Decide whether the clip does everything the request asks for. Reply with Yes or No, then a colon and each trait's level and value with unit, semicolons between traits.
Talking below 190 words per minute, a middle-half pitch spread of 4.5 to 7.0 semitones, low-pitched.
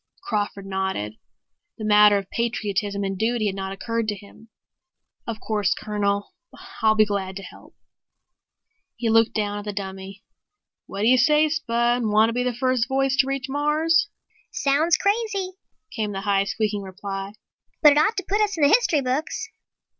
No: average, 175 wpm; average, 5.2 semitones; high, 220 Hz